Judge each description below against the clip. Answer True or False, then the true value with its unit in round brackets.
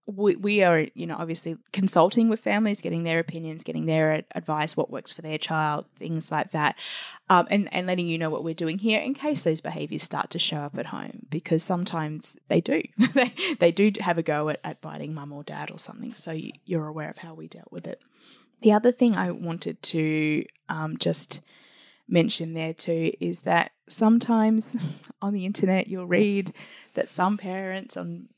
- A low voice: False (175 Hz)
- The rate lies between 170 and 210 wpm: True (200 wpm)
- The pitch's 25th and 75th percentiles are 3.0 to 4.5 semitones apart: False (5.0 semitones)